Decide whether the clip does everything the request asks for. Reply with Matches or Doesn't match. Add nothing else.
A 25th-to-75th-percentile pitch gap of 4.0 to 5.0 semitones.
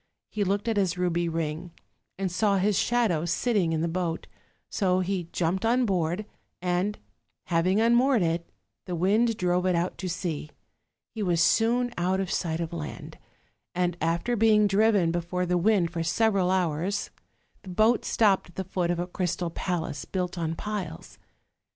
Doesn't match